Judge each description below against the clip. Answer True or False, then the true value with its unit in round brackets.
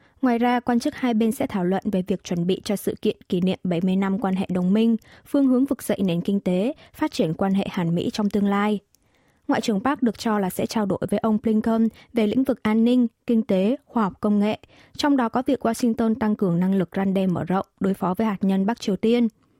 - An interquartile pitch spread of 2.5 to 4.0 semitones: True (3.5 semitones)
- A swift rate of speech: True (255 wpm)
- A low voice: False (215 Hz)